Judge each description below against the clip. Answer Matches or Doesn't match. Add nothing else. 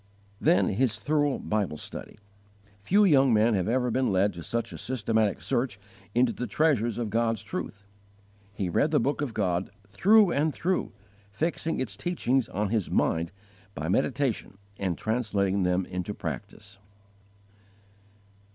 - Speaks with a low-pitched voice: Matches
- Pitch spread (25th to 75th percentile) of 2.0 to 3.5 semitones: Doesn't match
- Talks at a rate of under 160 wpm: Matches